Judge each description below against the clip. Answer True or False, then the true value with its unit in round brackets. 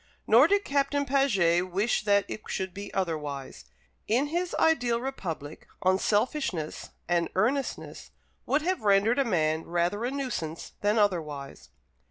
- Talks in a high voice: True (205 Hz)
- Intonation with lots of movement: True (7.8 semitones)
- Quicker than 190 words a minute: False (135 wpm)